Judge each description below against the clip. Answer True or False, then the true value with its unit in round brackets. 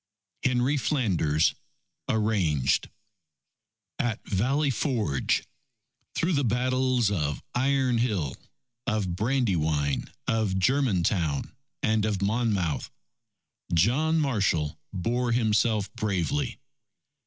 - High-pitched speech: False (110 Hz)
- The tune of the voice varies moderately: False (5.7 semitones)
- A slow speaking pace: True (85 wpm)